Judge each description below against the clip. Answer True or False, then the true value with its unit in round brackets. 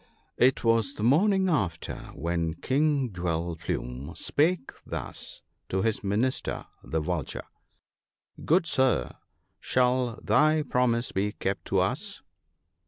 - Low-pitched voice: True (115 Hz)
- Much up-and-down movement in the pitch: True (7.8 semitones)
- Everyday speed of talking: False (125 wpm)